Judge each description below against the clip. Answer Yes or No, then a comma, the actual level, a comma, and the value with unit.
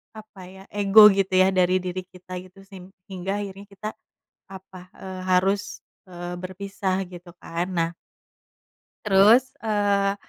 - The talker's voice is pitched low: No, high, 190 Hz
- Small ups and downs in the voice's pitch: Yes, narrow, 1.5 semitones